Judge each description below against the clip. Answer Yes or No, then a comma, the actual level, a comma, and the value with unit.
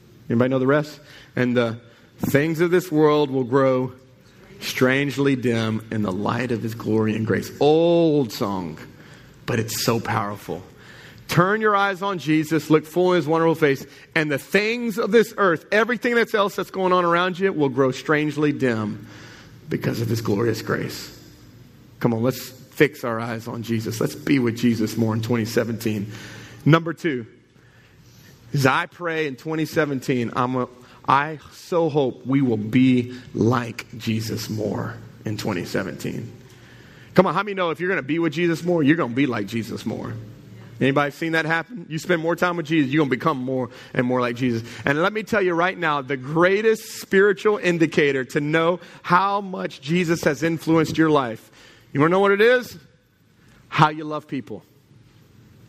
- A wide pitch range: Yes, wide, 5.8 semitones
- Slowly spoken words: No, average, 180 wpm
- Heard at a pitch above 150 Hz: No, medium, 140 Hz